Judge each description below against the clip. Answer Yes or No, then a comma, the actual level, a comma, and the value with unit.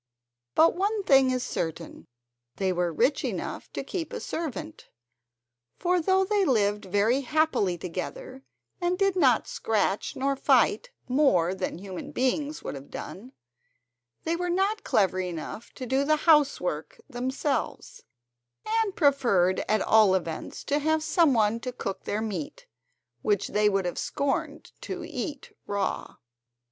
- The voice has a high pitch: Yes, very high, 255 Hz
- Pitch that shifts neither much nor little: No, wide, 8.4 semitones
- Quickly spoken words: No, average, 145 wpm